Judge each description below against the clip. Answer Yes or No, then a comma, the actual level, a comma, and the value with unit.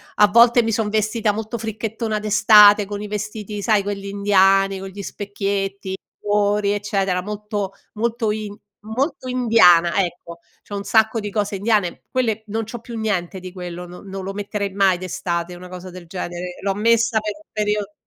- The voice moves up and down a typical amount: No, narrow, 2.1 semitones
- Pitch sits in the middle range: No, high, 205 Hz